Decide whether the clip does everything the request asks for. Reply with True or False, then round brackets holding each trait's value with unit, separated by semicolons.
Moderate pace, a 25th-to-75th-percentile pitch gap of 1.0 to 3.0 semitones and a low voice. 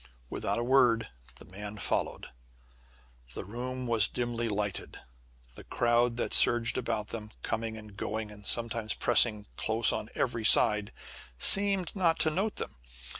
True (145 wpm; 2.4 semitones; 115 Hz)